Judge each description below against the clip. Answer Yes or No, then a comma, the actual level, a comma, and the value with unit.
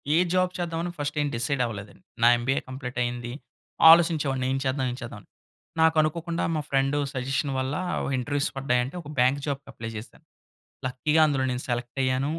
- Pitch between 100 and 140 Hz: Yes, low, 135 Hz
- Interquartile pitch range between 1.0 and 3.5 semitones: Yes, average, 3.2 semitones